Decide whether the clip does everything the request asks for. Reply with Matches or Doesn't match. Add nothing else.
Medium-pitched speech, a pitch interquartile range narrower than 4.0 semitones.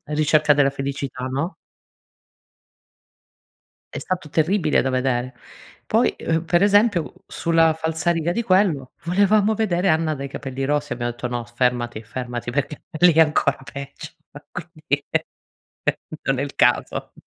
Doesn't match